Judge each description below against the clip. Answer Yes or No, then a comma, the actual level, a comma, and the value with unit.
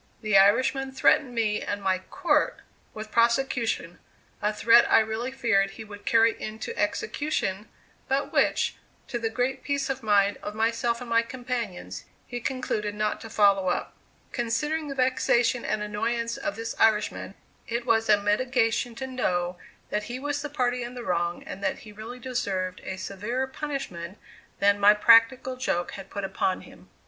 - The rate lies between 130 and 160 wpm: No, average, 170 wpm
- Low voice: No, high, 230 Hz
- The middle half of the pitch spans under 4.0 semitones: Yes, average, 3.6 semitones